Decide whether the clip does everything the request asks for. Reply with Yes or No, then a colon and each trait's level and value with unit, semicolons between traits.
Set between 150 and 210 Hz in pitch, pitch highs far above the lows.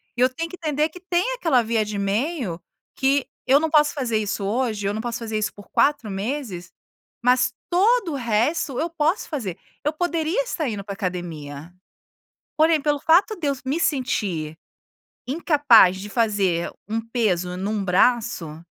No: high, 245 Hz; wide, 7.3 semitones